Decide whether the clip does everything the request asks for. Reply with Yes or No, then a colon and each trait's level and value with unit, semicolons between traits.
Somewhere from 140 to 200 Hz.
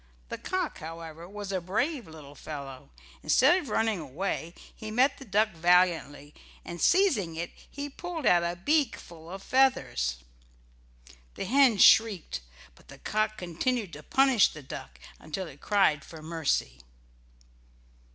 Yes: medium, 185 Hz